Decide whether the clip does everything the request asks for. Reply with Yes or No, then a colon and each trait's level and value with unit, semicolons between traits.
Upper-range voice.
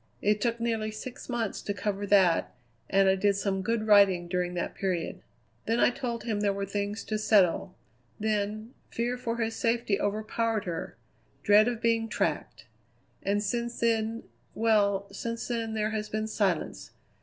Yes: high, 215 Hz